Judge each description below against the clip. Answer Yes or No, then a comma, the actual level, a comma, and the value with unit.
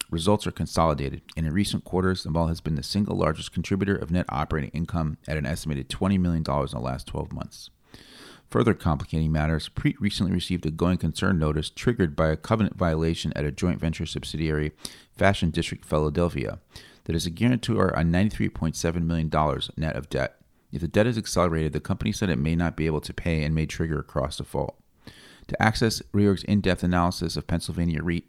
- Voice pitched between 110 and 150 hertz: No, very low, 85 Hz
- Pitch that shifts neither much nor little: Yes, average, 3.3 semitones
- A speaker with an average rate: Yes, average, 195 wpm